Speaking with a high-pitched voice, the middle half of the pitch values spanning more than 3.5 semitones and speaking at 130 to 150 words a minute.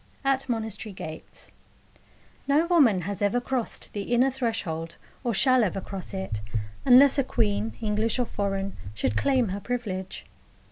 Yes: high, 220 Hz; average, 5.0 semitones; average, 145 wpm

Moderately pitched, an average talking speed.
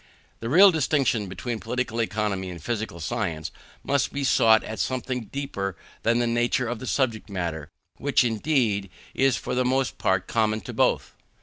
No: low, 115 Hz; average, 170 wpm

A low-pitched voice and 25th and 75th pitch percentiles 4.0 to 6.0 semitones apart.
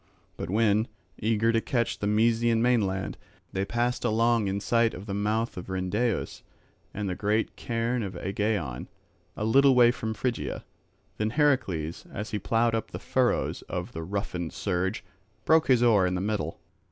No: low, 110 Hz; average, 3.3 semitones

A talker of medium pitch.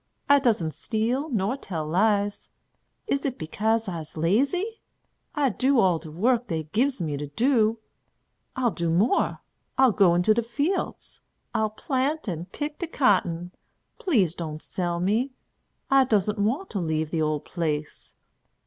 No: high, 210 Hz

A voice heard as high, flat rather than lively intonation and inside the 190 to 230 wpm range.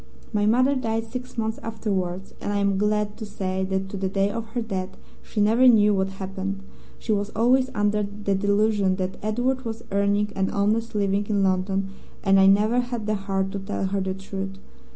Yes: high, 205 Hz; narrow, 2.3 semitones; average, 200 wpm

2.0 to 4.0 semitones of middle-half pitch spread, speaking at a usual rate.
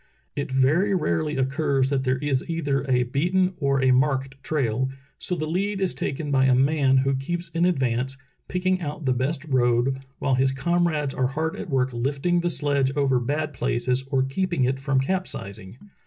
Yes: average, 3.4 semitones; average, 185 wpm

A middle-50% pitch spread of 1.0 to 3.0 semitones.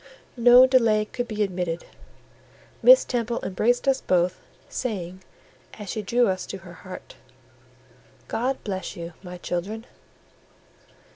No: average, 4.9 semitones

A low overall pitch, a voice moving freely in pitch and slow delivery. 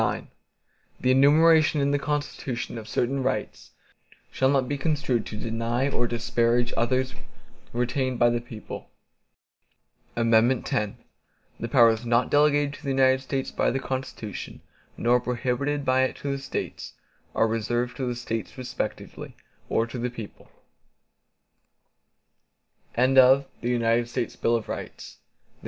No: low, 125 Hz; narrow, 2.6 semitones; slow, 120 wpm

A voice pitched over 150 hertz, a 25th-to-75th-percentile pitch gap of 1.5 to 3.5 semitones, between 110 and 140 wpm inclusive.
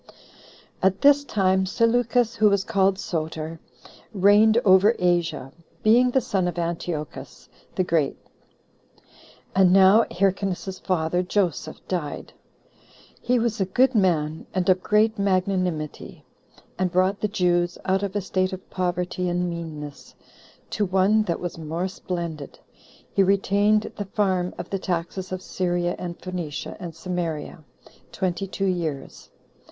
Yes: medium, 185 Hz; narrow, 2.4 semitones; slow, 135 wpm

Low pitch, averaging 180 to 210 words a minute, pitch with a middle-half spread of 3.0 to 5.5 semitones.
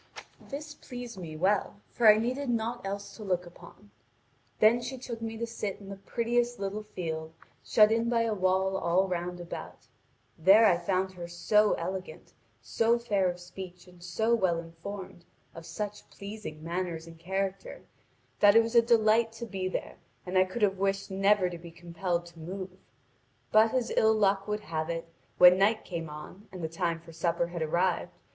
No: high, 190 Hz; average, 190 wpm; average, 4.0 semitones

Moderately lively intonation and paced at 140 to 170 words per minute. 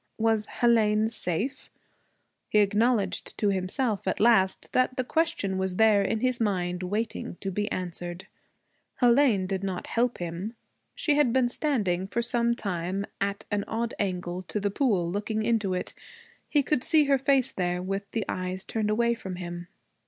Yes: average, 4.0 semitones; average, 165 wpm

